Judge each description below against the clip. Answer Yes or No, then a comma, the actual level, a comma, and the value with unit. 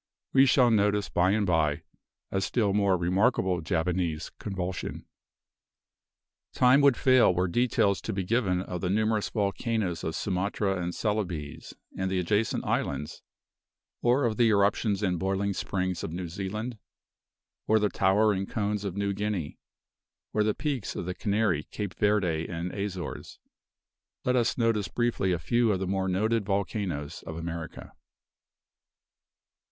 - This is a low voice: Yes, low, 100 Hz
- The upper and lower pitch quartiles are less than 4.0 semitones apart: Yes, average, 3.1 semitones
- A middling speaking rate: Yes, average, 145 wpm